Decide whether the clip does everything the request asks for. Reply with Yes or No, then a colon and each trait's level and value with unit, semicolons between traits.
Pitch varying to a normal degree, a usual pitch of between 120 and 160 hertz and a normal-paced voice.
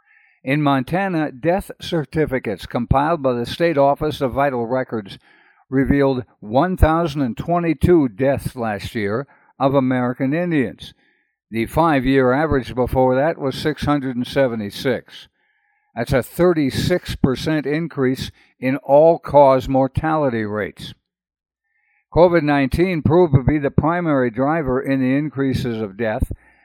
No: average, 3.7 semitones; medium, 140 Hz; slow, 115 wpm